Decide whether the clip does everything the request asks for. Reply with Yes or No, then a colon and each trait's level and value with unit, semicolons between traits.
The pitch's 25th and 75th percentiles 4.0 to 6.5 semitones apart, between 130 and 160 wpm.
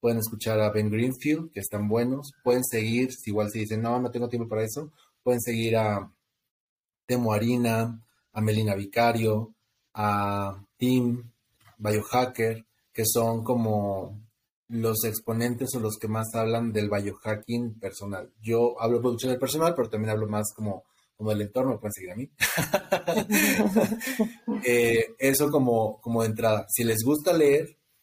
No: narrow, 2.5 semitones; average, 150 wpm